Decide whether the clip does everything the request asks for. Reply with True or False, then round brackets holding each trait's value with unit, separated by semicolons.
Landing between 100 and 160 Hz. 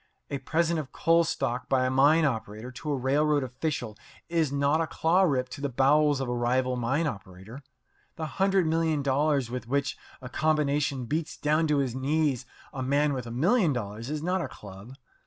True (140 Hz)